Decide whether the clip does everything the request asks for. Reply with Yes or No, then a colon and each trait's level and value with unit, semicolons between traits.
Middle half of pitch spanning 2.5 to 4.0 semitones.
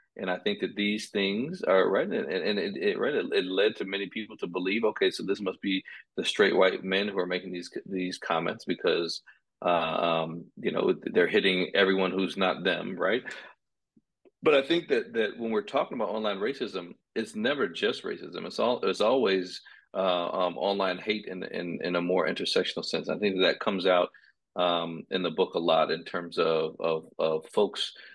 Yes: average, 2.9 semitones